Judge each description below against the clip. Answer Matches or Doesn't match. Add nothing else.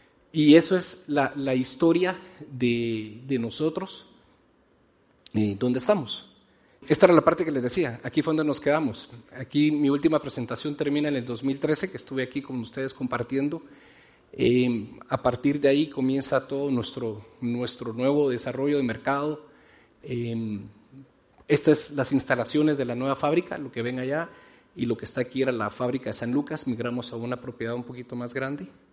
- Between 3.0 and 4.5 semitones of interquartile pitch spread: Matches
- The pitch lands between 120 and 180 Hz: Matches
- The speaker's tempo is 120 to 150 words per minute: Doesn't match